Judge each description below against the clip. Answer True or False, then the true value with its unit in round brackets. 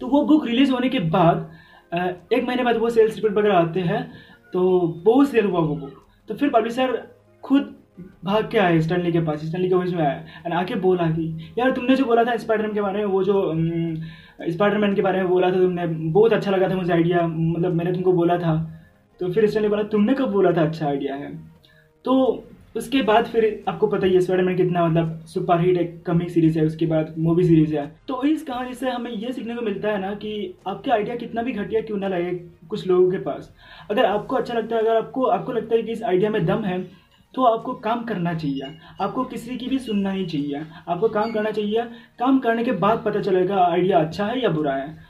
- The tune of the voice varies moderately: True (4.8 semitones)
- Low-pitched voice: False (190 Hz)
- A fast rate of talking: True (225 wpm)